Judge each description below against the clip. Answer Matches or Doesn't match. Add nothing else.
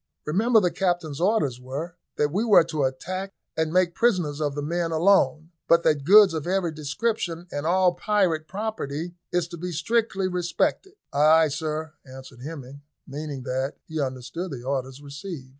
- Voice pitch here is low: Doesn't match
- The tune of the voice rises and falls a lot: Doesn't match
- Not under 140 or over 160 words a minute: Doesn't match